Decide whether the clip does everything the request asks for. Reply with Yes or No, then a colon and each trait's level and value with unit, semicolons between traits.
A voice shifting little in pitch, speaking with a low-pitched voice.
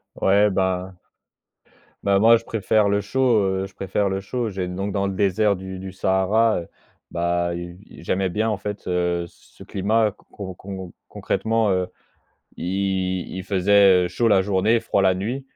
Yes: narrow, 2.1 semitones; very low, 95 Hz